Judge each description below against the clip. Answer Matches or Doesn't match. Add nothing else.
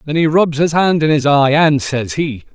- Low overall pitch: Doesn't match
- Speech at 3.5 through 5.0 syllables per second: Matches